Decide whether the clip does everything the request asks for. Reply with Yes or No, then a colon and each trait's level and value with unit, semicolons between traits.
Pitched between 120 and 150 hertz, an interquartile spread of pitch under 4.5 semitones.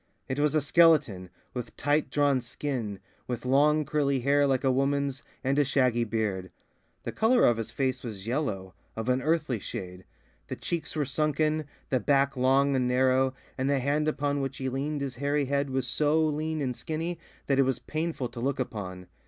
Yes: low, 135 Hz; average, 2.8 semitones